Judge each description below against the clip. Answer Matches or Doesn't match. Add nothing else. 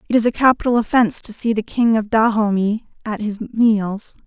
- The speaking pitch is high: Matches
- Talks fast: Doesn't match